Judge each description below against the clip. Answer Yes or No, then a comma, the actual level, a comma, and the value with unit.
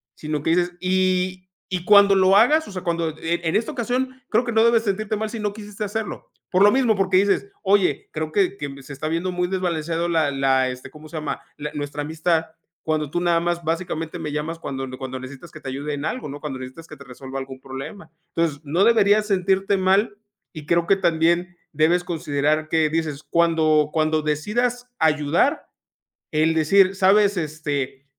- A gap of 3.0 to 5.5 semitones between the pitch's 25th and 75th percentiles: Yes, average, 4.4 semitones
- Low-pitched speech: No, medium, 170 Hz